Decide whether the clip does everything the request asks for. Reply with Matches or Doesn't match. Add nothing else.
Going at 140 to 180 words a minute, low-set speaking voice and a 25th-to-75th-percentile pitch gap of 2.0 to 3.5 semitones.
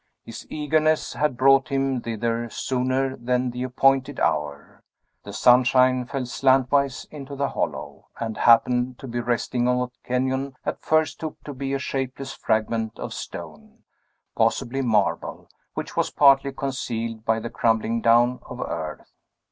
Matches